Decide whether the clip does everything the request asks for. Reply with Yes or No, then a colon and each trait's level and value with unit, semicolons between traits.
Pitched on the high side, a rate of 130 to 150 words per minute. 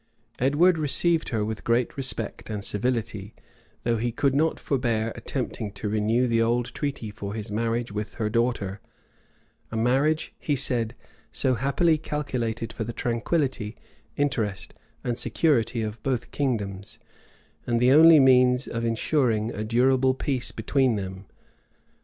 No: low, 120 Hz; average, 140 wpm